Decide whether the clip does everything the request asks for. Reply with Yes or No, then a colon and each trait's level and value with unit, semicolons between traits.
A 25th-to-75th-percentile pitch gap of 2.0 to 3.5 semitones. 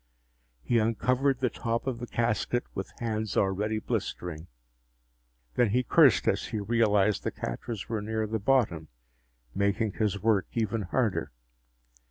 Yes: average, 2.7 semitones